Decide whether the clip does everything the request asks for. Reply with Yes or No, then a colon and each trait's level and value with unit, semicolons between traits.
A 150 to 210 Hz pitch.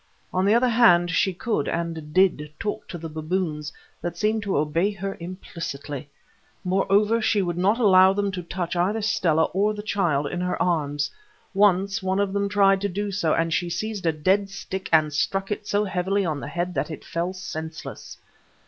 Yes: medium, 185 Hz